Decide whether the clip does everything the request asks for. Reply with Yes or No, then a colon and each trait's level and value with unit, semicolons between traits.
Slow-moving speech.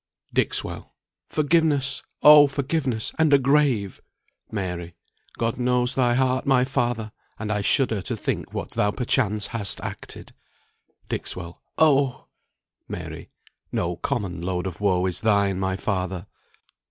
Yes: slow, 130 wpm